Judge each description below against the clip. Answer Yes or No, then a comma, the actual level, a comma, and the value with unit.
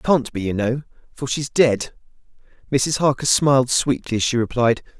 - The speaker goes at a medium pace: Yes, average, 180 wpm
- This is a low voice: Yes, low, 130 Hz